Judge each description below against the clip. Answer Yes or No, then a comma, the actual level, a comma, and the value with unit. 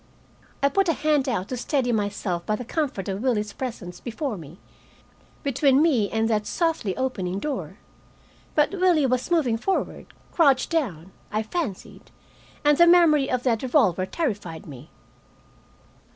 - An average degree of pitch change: No, wide, 6.5 semitones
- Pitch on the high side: Yes, very high, 250 Hz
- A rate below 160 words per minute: Yes, average, 150 wpm